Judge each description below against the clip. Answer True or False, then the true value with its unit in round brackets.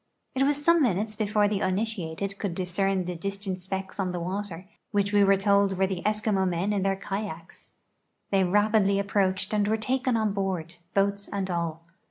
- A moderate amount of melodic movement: False (1.9 semitones)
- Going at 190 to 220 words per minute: True (195 wpm)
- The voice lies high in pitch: True (195 Hz)